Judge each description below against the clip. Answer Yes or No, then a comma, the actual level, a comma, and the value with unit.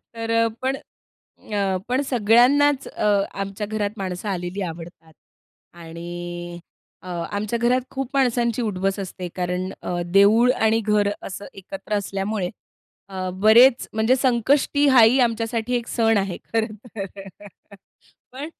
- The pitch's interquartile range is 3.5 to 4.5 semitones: Yes, average, 4.2 semitones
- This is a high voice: Yes, high, 215 Hz